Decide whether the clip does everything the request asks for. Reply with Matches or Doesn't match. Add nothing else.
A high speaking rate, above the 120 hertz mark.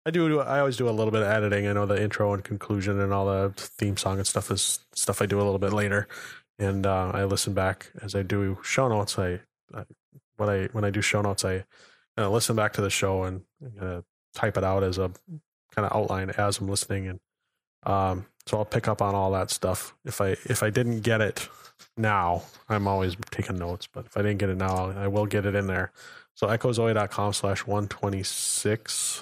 Doesn't match